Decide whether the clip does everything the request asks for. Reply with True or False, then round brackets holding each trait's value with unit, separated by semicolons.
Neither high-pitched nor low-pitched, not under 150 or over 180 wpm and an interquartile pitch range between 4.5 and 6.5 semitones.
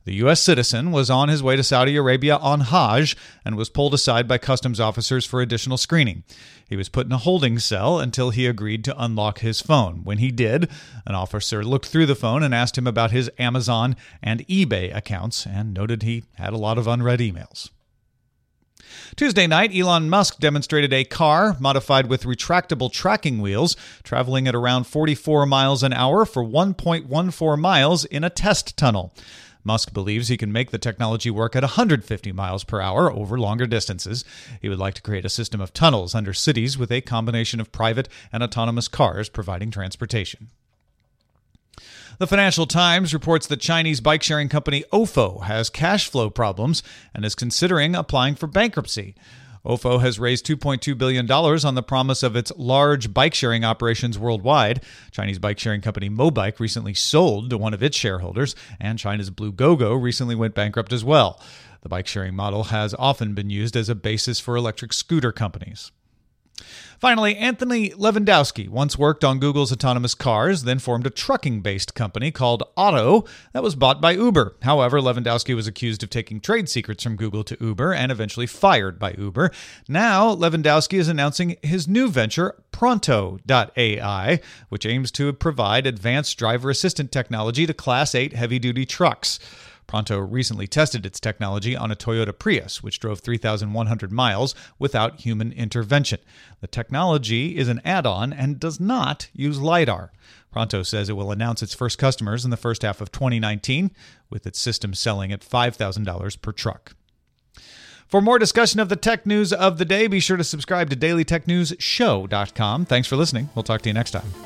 False (125 Hz; 170 wpm; 5.2 semitones)